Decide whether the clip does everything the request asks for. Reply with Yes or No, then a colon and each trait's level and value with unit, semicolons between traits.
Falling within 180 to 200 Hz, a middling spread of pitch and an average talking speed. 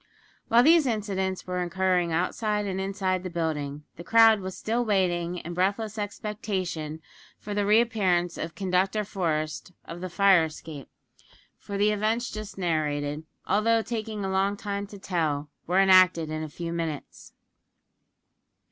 Yes: high, 190 Hz; average, 3.6 semitones; average, 150 wpm